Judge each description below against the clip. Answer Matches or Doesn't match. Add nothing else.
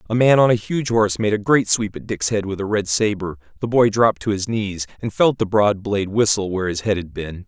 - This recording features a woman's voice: Doesn't match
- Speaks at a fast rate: Matches